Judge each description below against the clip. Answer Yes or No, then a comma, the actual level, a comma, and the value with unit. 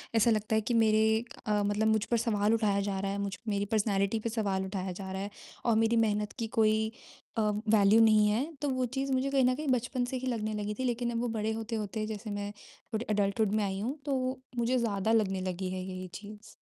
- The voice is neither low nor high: No, high, 215 Hz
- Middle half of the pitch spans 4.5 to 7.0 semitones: No, narrow, 2.4 semitones